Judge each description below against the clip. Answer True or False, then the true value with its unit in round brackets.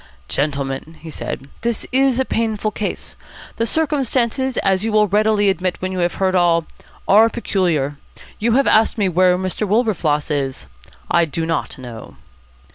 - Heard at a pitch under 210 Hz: True (190 Hz)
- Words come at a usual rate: True (160 wpm)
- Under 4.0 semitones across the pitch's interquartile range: False (5.4 semitones)